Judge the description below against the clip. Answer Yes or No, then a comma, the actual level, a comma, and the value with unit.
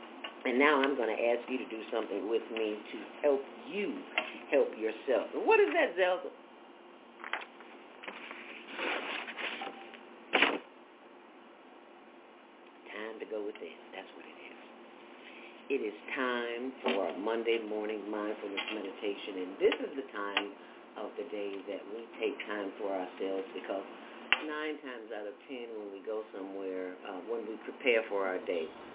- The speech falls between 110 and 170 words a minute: Yes, average, 145 wpm